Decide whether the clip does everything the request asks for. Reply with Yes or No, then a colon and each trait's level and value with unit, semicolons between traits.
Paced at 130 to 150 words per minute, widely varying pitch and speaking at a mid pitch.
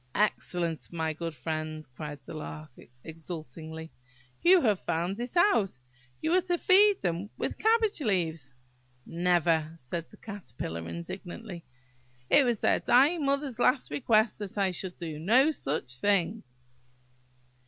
Yes: average, 140 wpm; wide, 7.3 semitones; medium, 180 Hz